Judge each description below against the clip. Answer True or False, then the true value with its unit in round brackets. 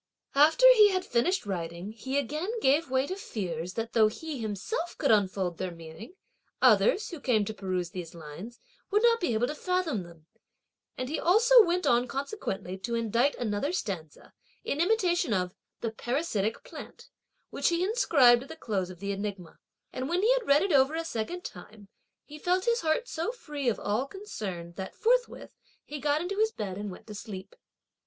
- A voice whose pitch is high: True (255 Hz)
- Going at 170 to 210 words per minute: True (190 wpm)